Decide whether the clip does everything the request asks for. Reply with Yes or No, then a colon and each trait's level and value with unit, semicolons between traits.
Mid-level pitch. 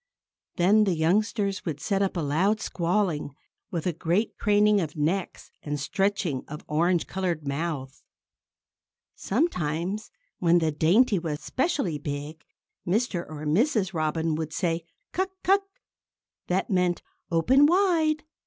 Yes: medium, 175 Hz